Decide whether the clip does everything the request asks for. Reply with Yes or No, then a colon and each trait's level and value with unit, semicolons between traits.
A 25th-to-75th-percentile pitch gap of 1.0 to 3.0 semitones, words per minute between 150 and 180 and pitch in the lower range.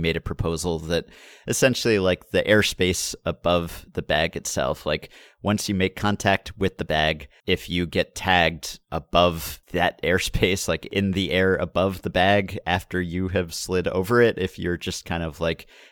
Yes: narrow, 2.4 semitones; average, 175 wpm; very low, 90 Hz